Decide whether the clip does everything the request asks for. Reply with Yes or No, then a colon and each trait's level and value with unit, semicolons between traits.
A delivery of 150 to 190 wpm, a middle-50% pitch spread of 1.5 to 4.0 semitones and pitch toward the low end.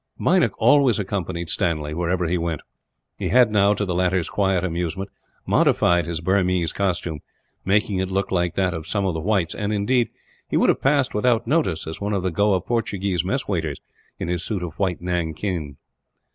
Yes: average, 185 wpm; average, 3.1 semitones; very low, 95 Hz